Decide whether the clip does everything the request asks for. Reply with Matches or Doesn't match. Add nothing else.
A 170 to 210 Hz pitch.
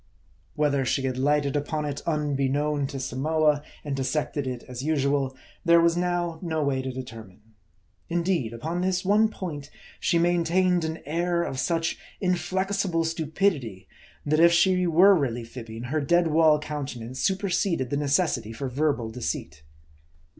Doesn't match